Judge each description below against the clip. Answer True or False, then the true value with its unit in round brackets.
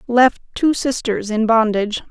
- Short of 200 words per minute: True (140 wpm)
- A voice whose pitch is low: False (230 Hz)